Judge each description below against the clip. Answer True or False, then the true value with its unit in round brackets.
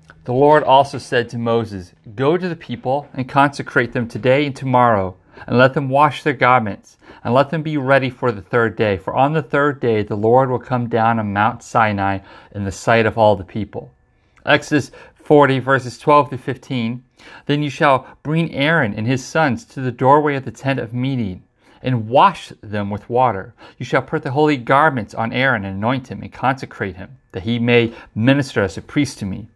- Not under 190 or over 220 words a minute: True (205 wpm)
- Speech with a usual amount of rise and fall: True (3.7 semitones)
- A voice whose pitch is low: True (125 Hz)